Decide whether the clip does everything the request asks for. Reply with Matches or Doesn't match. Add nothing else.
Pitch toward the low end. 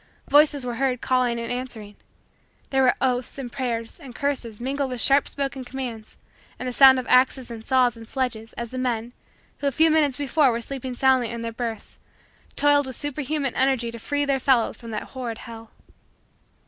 Doesn't match